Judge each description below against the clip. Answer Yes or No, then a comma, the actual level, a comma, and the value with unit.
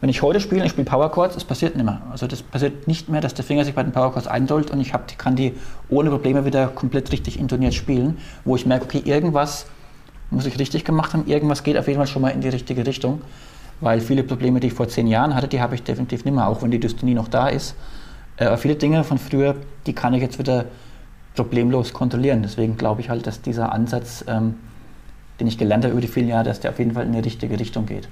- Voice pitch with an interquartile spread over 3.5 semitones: No, average, 2.8 semitones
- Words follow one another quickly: Yes, fast, 255 wpm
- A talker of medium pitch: No, low, 130 Hz